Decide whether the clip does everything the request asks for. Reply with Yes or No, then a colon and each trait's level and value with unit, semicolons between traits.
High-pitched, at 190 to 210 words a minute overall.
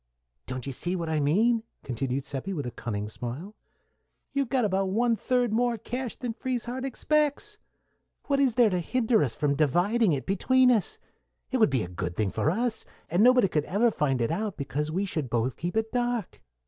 Yes: high, 195 Hz; average, 200 wpm